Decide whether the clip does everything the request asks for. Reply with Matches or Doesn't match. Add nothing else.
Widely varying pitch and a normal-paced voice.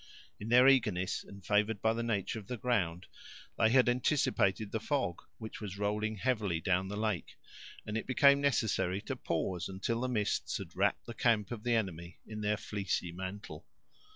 Doesn't match